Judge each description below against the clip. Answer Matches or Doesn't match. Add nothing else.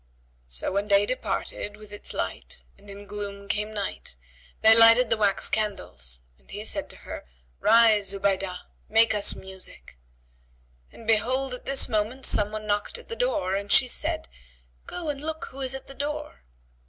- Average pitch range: Matches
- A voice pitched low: Doesn't match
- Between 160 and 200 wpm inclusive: Matches